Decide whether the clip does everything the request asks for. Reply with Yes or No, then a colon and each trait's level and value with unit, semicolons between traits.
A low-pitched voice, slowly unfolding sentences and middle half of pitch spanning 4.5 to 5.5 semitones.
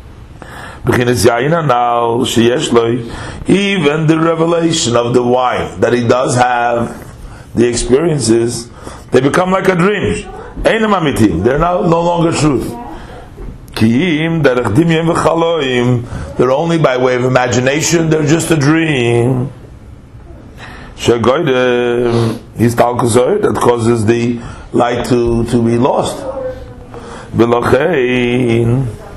Yes: low, 125 Hz; slow, 85 wpm; average, 4.9 semitones